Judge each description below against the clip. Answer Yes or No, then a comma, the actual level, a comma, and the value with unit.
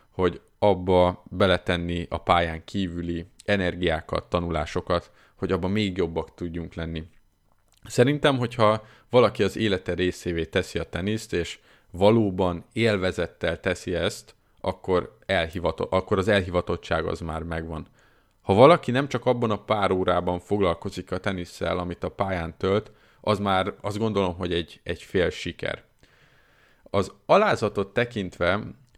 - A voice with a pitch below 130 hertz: Yes, very low, 95 Hz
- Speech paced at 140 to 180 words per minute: No, average, 130 wpm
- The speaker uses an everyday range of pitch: Yes, average, 3.3 semitones